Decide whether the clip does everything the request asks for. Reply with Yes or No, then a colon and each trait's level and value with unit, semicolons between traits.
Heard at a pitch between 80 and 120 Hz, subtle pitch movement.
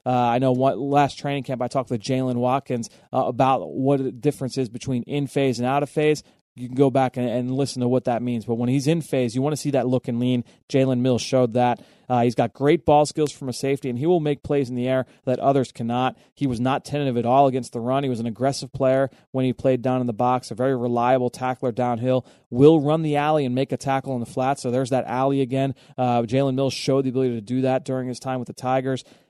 No: low, 130 Hz; narrow, 1.7 semitones